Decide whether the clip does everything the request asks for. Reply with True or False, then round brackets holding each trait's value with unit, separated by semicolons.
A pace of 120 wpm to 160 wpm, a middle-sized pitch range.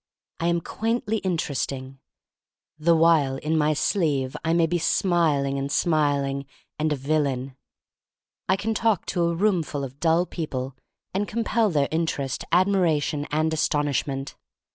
True (155 wpm; 3.8 semitones)